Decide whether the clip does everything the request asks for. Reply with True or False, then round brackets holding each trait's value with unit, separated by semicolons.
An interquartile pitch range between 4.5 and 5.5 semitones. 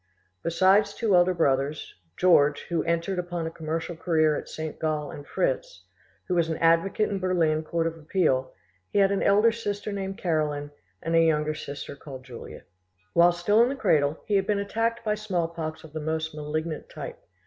False (4.0 semitones)